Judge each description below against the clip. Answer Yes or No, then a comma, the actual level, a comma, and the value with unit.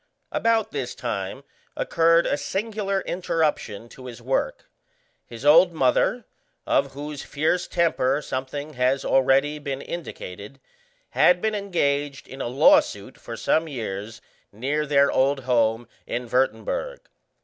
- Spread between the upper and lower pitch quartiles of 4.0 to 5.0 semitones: Yes, average, 4.7 semitones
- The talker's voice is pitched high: No, medium, 140 Hz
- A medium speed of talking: No, slow, 130 wpm